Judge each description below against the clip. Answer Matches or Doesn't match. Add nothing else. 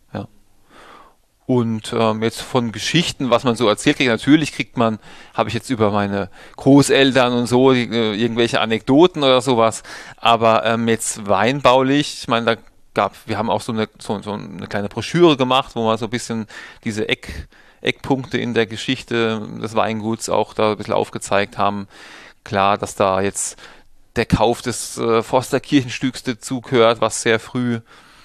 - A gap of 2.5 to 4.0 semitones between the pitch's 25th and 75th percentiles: Matches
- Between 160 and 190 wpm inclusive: Matches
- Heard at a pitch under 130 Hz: Matches